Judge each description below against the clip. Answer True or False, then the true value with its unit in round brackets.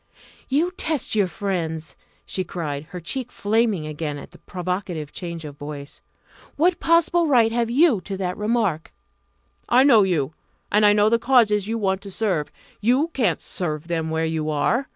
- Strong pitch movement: True (6.5 semitones)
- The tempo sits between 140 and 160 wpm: False (175 wpm)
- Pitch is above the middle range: True (195 Hz)